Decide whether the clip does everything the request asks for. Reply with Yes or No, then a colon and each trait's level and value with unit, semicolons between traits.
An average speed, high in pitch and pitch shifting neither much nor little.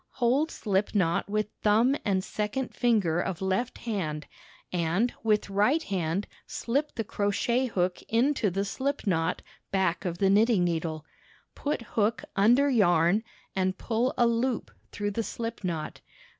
Yes: average, 145 wpm; high, 205 Hz; average, 4.2 semitones